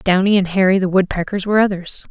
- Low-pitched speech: No, high, 190 Hz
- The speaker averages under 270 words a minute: Yes, average, 200 wpm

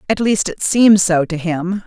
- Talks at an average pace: No, fast, 225 wpm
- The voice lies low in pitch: No, high, 190 Hz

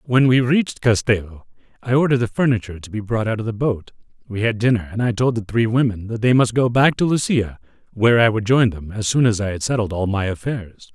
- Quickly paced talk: Yes, fast, 245 wpm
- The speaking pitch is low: Yes, low, 115 Hz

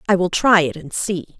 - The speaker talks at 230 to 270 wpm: Yes, fast, 260 wpm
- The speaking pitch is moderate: Yes, medium, 180 Hz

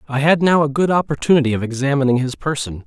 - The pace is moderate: No, fast, 210 wpm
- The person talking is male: Yes, male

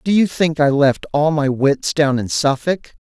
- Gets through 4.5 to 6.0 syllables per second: No, 4.3 syllables/s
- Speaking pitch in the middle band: Yes, medium, 150 Hz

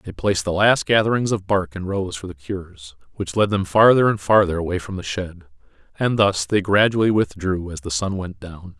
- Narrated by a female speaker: No, male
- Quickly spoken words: Yes, fast, 220 wpm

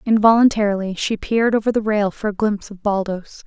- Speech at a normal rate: Yes, average, 190 wpm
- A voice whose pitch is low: No, high, 210 Hz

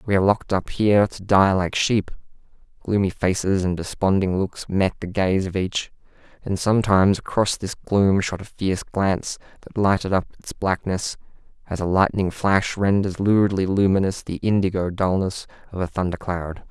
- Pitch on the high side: No, very low, 95 Hz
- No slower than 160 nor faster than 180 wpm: Yes, average, 170 wpm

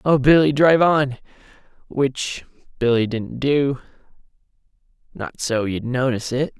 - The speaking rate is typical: No, slow, 120 wpm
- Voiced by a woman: No, male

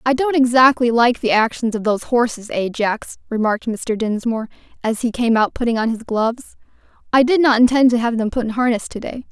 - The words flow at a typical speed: No, fast, 215 wpm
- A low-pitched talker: No, high, 235 Hz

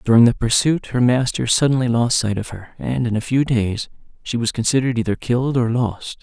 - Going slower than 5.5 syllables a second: No, 5.6 syllables/s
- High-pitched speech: No, low, 120 Hz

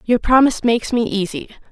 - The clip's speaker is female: Yes, female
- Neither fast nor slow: Yes, average, 175 wpm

